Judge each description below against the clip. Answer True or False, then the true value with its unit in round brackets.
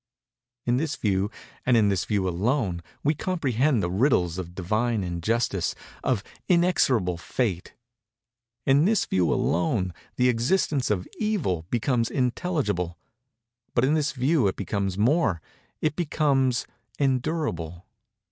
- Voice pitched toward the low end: True (120 Hz)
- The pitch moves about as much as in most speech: False (7.5 semitones)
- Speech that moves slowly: True (120 wpm)